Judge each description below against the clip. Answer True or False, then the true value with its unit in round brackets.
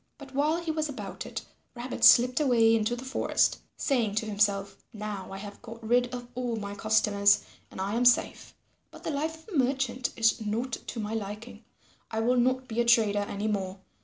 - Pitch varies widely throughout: False (3.2 semitones)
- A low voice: False (230 Hz)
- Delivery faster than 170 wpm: True (200 wpm)